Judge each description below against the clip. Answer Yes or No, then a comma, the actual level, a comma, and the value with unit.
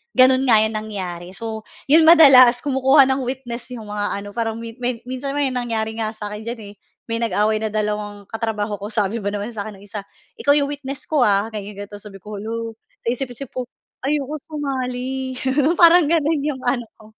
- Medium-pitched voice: No, high, 230 Hz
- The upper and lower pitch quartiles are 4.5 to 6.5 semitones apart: No, average, 4.0 semitones